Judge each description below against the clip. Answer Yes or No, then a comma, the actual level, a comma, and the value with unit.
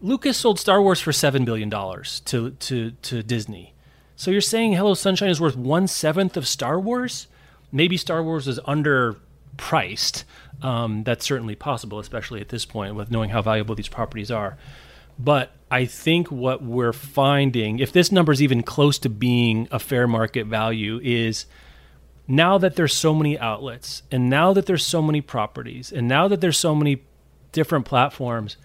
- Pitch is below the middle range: Yes, low, 130 Hz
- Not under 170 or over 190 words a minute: Yes, average, 175 wpm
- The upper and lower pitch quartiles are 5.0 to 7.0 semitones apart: Yes, wide, 5.6 semitones